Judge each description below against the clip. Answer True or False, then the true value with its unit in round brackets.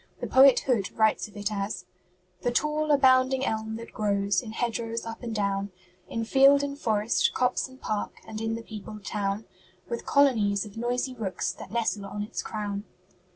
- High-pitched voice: True (225 Hz)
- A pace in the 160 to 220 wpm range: True (180 wpm)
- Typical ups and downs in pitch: True (3.6 semitones)